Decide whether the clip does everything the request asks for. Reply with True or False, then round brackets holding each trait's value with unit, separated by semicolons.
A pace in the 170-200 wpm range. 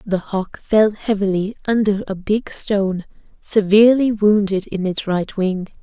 False (145 wpm)